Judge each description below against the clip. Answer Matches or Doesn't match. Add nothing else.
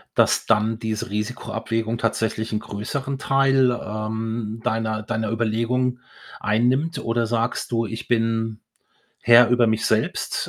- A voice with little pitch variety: Matches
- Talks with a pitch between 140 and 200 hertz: Doesn't match